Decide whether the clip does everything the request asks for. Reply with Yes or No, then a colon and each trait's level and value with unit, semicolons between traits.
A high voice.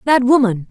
Yes: high, 240 Hz